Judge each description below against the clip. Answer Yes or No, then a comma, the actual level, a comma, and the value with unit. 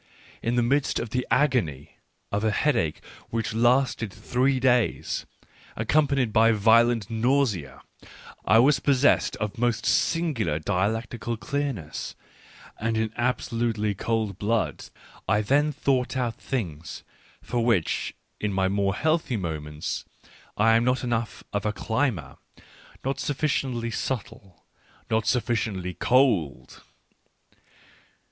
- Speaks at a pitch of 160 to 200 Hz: No, low, 115 Hz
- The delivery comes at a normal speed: No, slow, 115 wpm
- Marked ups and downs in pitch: No, average, 3.8 semitones